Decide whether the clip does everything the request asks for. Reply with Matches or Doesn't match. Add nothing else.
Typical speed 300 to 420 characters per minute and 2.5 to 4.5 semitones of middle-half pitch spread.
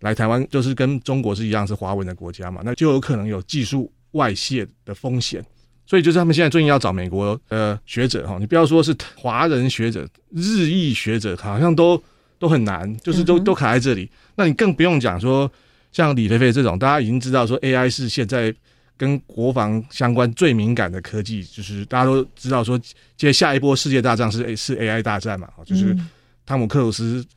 Matches